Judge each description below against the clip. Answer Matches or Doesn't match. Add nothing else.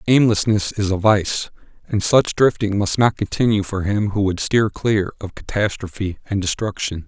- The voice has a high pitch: Doesn't match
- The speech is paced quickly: Doesn't match